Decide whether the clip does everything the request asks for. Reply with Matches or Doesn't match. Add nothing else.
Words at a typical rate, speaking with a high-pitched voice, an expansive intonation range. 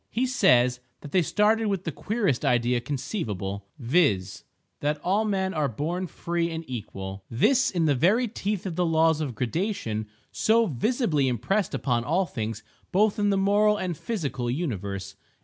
Doesn't match